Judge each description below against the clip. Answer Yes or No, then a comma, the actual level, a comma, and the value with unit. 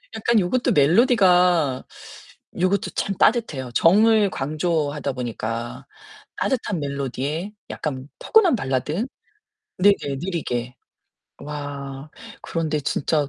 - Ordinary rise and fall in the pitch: No, wide, 6.3 semitones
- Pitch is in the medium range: Yes, medium, 155 Hz